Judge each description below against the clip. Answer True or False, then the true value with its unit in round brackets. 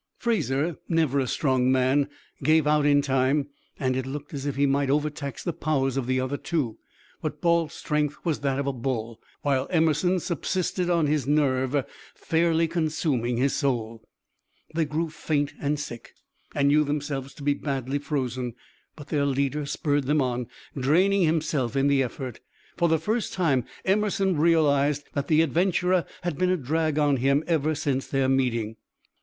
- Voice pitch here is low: False (145 Hz)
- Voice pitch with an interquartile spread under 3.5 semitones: True (3.1 semitones)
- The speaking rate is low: False (170 wpm)